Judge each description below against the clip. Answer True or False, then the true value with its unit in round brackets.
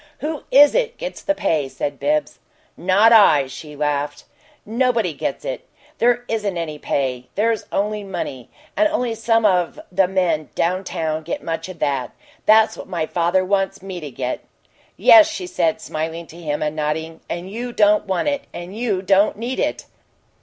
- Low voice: False (185 Hz)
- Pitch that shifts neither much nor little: False (6.3 semitones)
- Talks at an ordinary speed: True (175 wpm)